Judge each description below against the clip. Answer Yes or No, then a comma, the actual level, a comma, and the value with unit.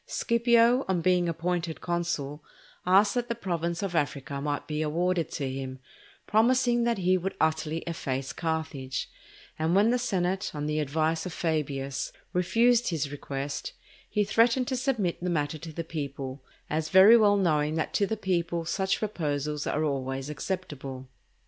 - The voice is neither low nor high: Yes, medium, 165 Hz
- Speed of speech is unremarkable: Yes, average, 160 wpm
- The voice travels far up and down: No, average, 4.8 semitones